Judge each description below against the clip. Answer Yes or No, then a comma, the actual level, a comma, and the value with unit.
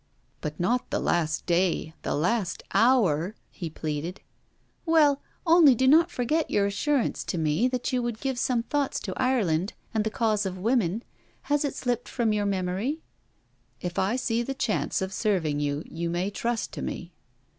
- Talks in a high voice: Yes, high, 215 Hz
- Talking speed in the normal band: Yes, average, 175 wpm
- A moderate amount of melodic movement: No, wide, 6.3 semitones